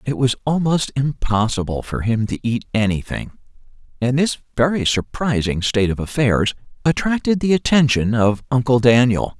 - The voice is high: No, low, 125 Hz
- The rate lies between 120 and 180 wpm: Yes, average, 140 wpm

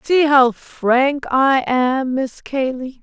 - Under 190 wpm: Yes, average, 140 wpm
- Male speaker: No, female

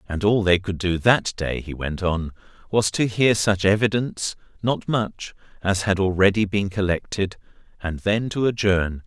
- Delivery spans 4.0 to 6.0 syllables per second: Yes, 4.5 syllables/s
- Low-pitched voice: Yes, low, 100 Hz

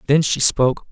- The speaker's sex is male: Yes, male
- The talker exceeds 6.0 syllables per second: No, 5.6 syllables/s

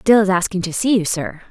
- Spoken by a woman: Yes, female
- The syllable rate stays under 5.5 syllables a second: No, 6.0 syllables/s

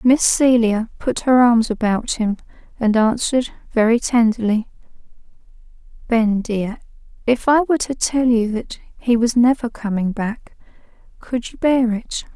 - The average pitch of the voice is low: No, high, 235 Hz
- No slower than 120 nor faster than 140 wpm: Yes, slow, 135 wpm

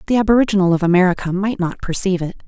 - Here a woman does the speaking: Yes, female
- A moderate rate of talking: Yes, average, 195 wpm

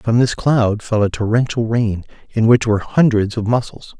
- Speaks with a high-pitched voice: No, low, 115 Hz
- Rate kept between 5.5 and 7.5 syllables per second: No, 4.9 syllables/s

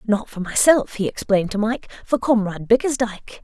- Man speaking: No, female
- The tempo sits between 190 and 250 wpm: No, average, 175 wpm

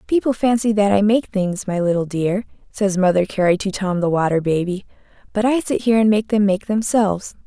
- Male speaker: No, female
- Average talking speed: No, fast, 210 wpm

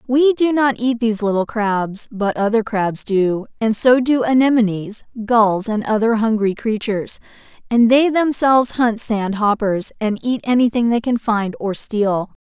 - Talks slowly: No, average, 165 wpm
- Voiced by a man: No, female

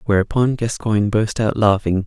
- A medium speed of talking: Yes, average, 145 wpm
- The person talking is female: No, male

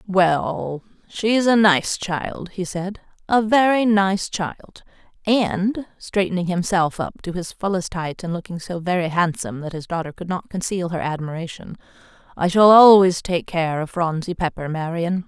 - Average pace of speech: Yes, average, 160 wpm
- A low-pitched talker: No, medium, 180 Hz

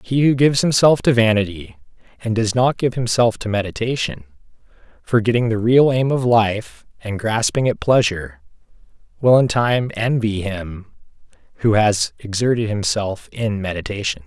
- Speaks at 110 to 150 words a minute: Yes, average, 145 wpm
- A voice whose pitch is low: Yes, low, 110 Hz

